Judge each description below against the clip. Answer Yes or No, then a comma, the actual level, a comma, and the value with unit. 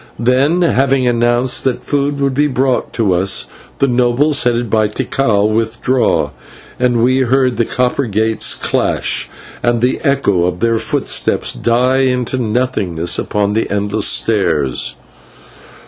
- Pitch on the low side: Yes, low, 120 Hz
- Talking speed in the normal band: No, slow, 130 wpm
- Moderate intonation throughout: Yes, average, 3.3 semitones